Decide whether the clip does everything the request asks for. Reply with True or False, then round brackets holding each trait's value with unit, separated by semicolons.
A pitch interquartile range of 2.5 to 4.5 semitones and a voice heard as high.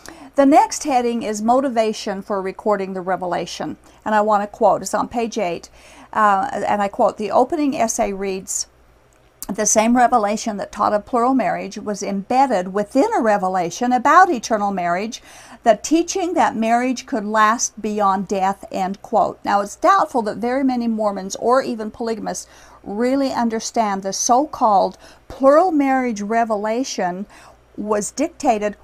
True (3.6 semitones; 225 Hz)